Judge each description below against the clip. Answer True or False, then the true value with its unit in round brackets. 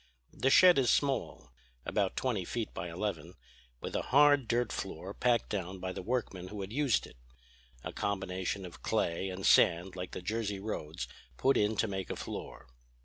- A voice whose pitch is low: True (100 Hz)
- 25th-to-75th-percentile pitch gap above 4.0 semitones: True (4.8 semitones)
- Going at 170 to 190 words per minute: True (180 wpm)